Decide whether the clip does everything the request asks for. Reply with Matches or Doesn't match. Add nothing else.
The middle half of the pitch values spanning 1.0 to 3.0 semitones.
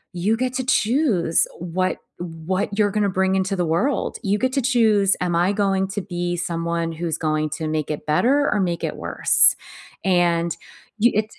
Doesn't match